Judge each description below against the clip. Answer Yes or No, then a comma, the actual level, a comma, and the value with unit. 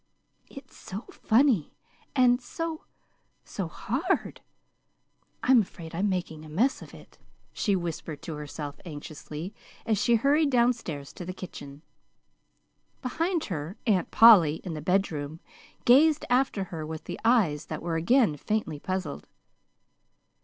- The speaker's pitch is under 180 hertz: No, medium, 185 Hz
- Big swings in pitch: Yes, wide, 7.6 semitones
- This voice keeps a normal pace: No, slow, 130 wpm